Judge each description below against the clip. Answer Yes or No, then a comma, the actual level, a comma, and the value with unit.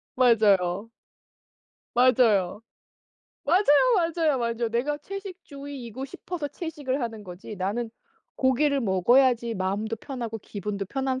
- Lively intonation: No, average, 4.9 semitones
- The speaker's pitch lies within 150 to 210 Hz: No, high, 240 Hz